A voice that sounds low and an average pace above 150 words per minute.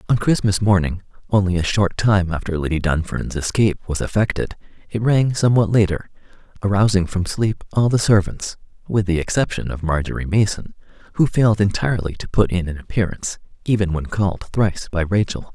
Yes: low, 100 Hz; average, 165 wpm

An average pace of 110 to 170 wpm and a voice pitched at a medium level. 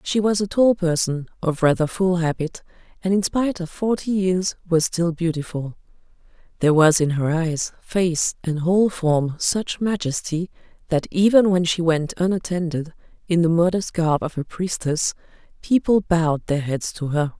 Yes: average, 165 wpm; medium, 170 Hz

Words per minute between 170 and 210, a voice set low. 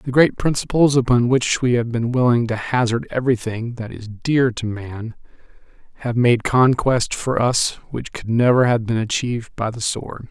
Yes: average, 180 wpm; low, 120 Hz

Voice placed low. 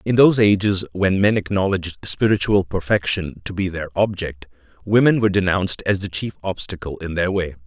Yes: very low, 95 Hz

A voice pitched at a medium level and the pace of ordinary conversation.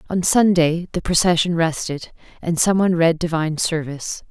Yes: medium, 170 Hz; average, 155 wpm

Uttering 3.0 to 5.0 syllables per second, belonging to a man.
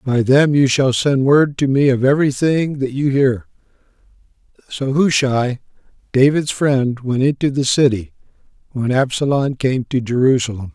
Yes: 4.6 syllables/s; male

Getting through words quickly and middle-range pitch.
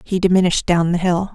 Yes: fast, 225 wpm; medium, 180 Hz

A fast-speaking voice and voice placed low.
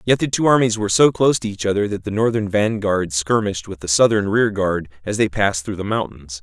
Yes: fast, 235 wpm; low, 105 Hz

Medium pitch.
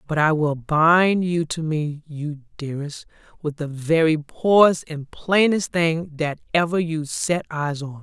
Yes: medium, 160 Hz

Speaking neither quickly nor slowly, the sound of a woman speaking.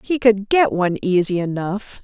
Yes: average, 175 wpm; female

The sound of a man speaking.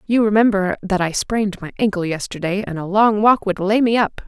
No: female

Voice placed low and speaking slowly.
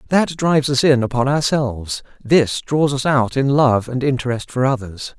No: low, 130 Hz; average, 185 wpm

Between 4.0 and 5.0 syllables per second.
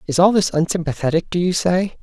No: 6.0 syllables/s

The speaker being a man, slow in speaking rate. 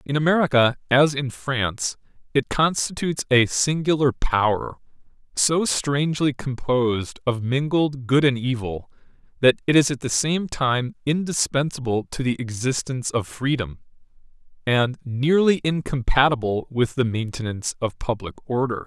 Yes: male; slow, 125 wpm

